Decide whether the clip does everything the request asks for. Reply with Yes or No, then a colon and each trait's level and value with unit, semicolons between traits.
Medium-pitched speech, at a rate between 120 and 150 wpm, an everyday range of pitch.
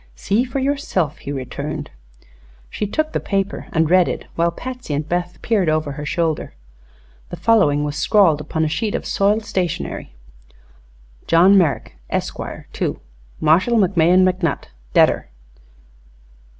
Yes: medium, 175 Hz; slow, 135 wpm; average, 4.8 semitones